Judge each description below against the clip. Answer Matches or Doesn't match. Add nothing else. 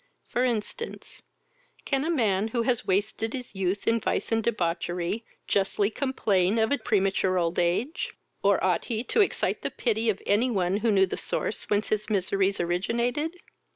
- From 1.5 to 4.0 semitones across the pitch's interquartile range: Matches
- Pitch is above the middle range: Matches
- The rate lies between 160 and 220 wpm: Matches